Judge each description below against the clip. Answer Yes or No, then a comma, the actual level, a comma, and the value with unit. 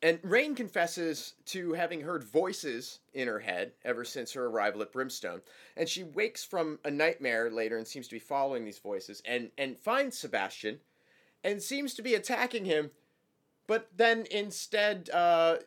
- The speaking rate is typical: Yes, average, 170 wpm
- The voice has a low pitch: No, medium, 165 Hz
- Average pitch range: No, wide, 7.9 semitones